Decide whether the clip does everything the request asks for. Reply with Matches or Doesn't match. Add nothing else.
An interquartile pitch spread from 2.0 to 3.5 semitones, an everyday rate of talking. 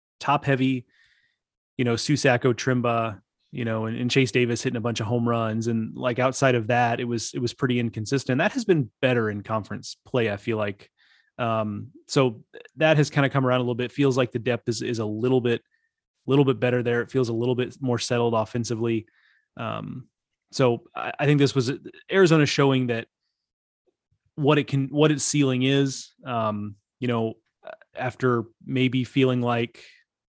Matches